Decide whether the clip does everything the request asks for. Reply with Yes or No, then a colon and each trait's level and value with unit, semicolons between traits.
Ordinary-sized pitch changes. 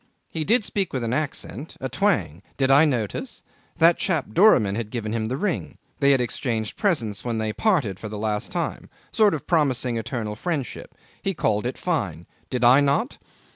No: wide, 6.8 semitones